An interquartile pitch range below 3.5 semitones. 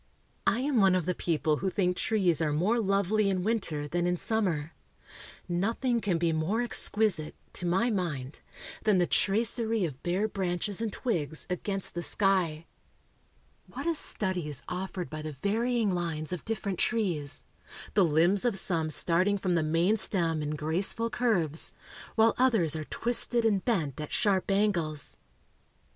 No: average, 4.8 semitones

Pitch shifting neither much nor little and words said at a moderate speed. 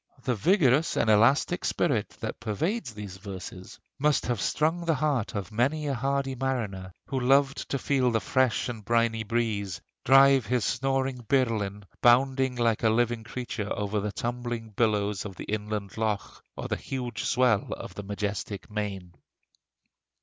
Yes: average, 4.2 semitones; average, 155 wpm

